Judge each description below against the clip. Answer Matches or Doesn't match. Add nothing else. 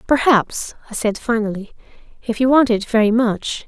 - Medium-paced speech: Matches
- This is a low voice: Doesn't match